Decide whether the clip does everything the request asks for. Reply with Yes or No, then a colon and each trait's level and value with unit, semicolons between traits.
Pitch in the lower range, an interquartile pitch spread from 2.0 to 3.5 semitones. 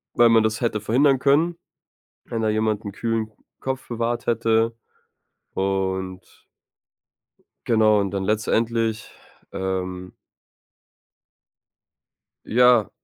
Yes: low, 110 Hz; average, 2.8 semitones